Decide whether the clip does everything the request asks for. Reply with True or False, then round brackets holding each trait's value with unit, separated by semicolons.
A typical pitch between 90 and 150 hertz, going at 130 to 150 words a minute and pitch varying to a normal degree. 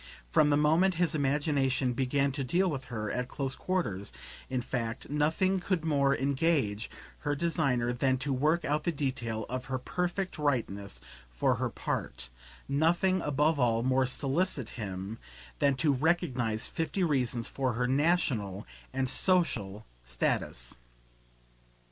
True (135 Hz; 140 wpm; 4.6 semitones)